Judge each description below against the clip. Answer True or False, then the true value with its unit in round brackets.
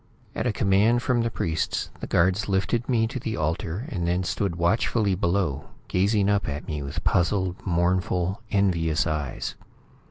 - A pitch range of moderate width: True (3.6 semitones)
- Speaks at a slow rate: False (160 wpm)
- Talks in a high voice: False (95 Hz)